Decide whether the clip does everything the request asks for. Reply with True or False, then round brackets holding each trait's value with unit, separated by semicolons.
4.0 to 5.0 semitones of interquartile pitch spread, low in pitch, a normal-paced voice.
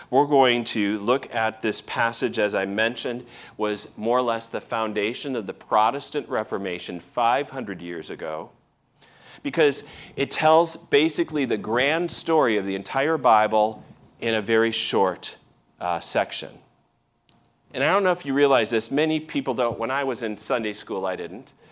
True (4.3 semitones; 115 Hz; 165 wpm)